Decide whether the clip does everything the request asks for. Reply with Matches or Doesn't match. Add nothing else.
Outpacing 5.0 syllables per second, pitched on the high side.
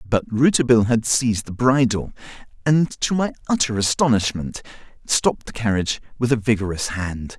Doesn't match